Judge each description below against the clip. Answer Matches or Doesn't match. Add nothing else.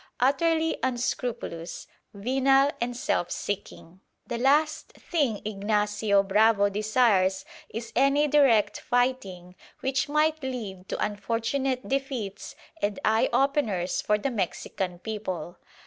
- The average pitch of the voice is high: Matches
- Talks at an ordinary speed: Doesn't match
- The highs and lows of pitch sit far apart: Doesn't match